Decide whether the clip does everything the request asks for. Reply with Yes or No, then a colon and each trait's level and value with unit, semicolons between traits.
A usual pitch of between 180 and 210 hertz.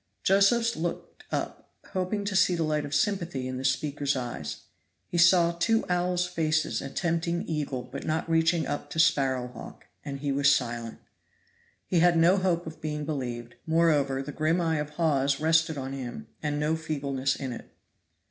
No: medium, 155 Hz